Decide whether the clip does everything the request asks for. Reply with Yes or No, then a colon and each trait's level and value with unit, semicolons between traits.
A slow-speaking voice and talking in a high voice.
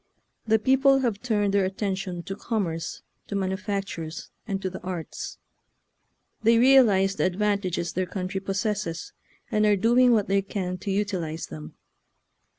No: average, 150 wpm; high, 195 Hz